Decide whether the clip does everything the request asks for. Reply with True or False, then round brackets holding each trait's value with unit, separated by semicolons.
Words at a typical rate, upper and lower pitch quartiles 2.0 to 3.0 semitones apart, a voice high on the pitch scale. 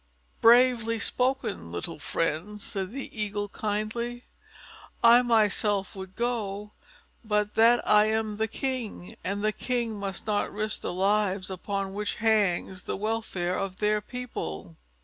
False (130 wpm; 2.7 semitones; 210 Hz)